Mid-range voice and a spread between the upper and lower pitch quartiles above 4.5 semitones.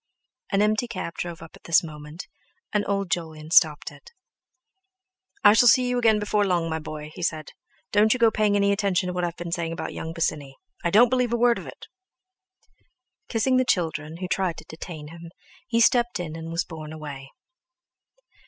Yes: medium, 175 Hz; average, 5.1 semitones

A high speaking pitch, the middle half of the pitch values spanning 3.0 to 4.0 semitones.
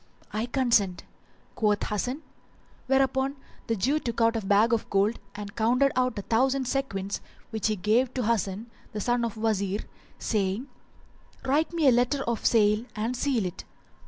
Yes: high, 230 Hz; average, 3.6 semitones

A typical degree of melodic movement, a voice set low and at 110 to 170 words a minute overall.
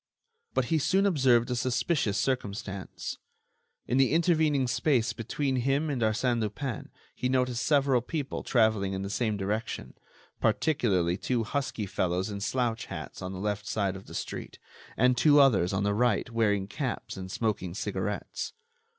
Yes: average, 4.7 semitones; low, 120 Hz; average, 160 wpm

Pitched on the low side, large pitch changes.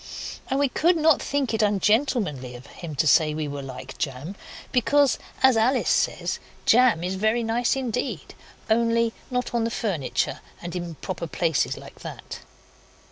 No: high, 220 Hz; wide, 7.3 semitones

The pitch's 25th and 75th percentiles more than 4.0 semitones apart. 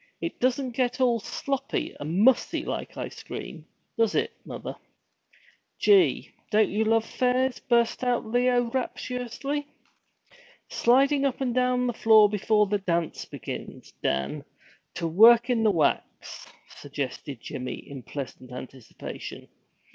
Yes: average, 4.5 semitones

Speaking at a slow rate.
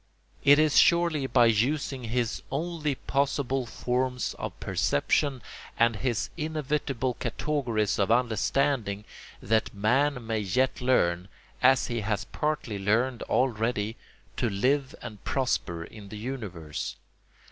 Yes: slow, 120 wpm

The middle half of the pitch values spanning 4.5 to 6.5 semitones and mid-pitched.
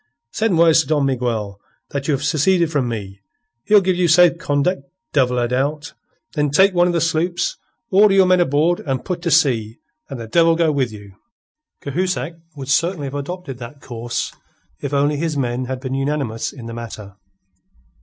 Yes: average, 5.2 semitones; medium, 145 Hz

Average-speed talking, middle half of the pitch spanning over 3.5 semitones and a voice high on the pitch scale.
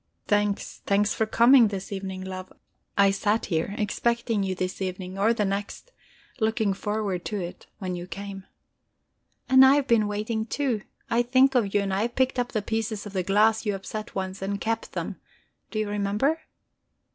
No: average, 185 wpm; narrow, 2.6 semitones; high, 205 Hz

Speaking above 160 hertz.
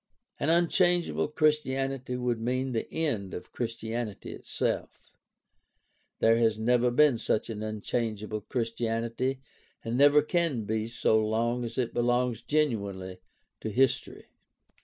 No: low, 120 Hz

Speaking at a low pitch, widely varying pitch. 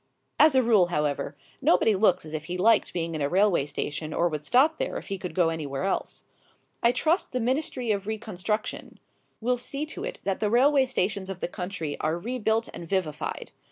No: high, 195 Hz; wide, 6.2 semitones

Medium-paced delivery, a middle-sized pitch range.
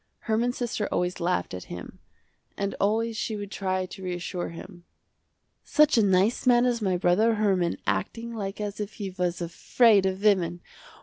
Yes: average, 170 wpm; average, 3.6 semitones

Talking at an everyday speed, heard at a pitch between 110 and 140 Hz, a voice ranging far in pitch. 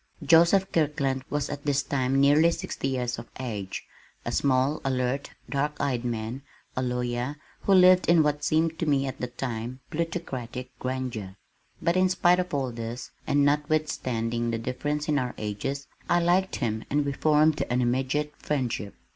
No: average, 165 wpm; low, 135 Hz; average, 3.5 semitones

